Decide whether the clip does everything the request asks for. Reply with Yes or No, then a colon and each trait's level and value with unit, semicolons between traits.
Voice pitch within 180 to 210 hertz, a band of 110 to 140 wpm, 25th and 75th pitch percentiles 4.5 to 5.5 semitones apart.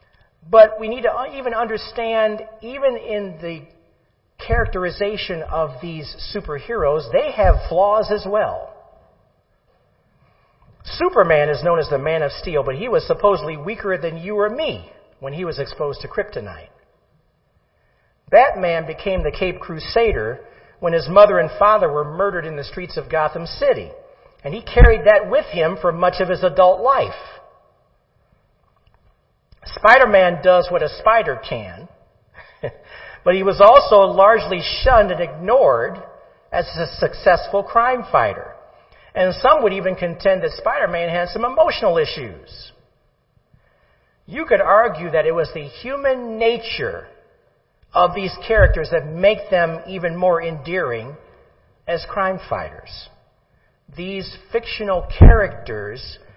Yes: high, 190 Hz; slow, 135 wpm; average, 5.0 semitones